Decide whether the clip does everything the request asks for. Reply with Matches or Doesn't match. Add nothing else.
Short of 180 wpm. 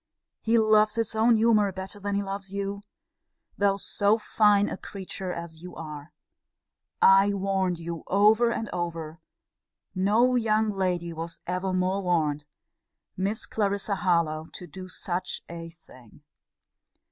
Matches